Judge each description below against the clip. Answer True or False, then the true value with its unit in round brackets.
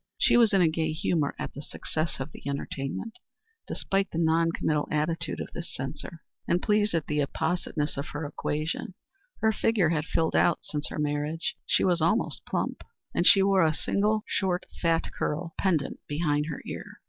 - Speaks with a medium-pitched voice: True (165 Hz)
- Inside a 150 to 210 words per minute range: True (185 wpm)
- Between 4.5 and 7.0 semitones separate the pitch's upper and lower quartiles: False (3.2 semitones)